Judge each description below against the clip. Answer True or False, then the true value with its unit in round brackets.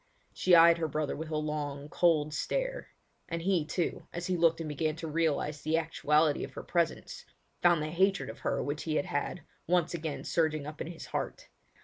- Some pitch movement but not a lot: False (2.2 semitones)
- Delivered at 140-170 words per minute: False (205 wpm)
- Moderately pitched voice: True (160 Hz)